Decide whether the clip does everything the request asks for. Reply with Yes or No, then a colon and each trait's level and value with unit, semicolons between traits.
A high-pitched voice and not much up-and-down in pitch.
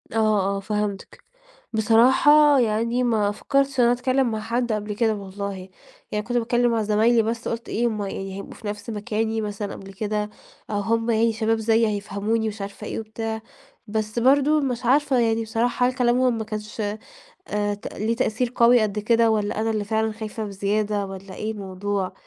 Yes: high, 220 Hz; narrow, 2.2 semitones